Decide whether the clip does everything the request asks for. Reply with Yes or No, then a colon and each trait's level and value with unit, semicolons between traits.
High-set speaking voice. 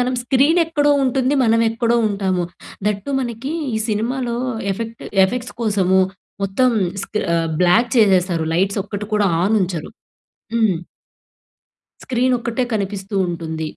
Yes: high, 220 Hz